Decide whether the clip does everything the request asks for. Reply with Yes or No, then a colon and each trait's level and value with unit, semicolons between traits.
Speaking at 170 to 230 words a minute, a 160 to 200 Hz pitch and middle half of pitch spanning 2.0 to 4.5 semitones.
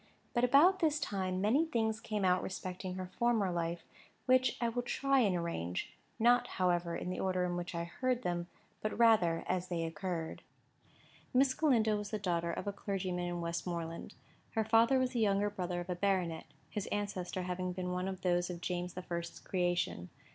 Yes: average, 190 wpm; medium, 185 Hz; average, 4.0 semitones